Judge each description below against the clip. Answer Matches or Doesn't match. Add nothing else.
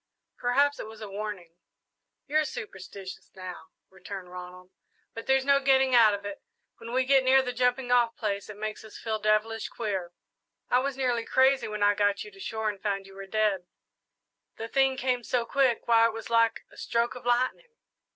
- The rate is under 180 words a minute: Doesn't match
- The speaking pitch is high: Matches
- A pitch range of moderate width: Matches